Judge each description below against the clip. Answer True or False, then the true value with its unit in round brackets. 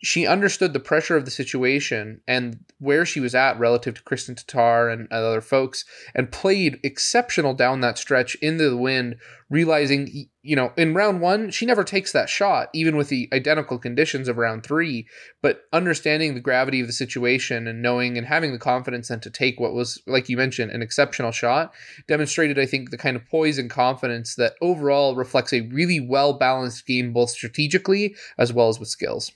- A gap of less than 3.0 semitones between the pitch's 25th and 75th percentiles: False (3.8 semitones)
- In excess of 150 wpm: True (190 wpm)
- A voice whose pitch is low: True (130 Hz)